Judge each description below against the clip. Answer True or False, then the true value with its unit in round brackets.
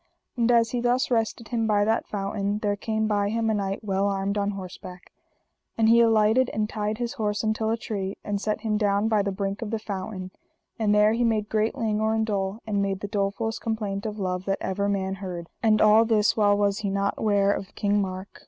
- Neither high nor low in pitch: False (210 Hz)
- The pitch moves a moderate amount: False (1.9 semitones)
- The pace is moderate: False (225 wpm)